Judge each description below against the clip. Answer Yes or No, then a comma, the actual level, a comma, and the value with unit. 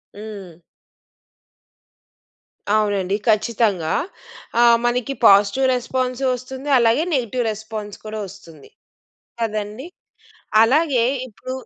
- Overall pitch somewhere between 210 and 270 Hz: Yes, high, 220 Hz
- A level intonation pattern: No, average, 3.5 semitones